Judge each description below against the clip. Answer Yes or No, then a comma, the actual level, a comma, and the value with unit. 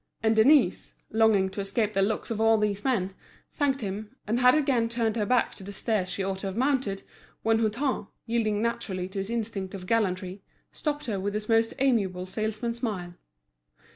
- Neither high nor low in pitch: No, high, 215 Hz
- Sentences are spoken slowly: No, average, 190 wpm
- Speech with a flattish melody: No, average, 3.1 semitones